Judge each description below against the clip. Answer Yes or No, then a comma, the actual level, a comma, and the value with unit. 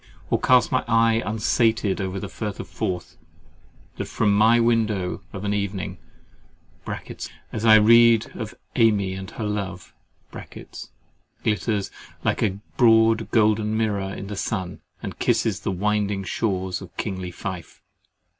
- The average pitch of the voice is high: No, low, 105 Hz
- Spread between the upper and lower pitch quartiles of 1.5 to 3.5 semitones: Yes, average, 2.7 semitones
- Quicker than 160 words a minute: No, slow, 135 wpm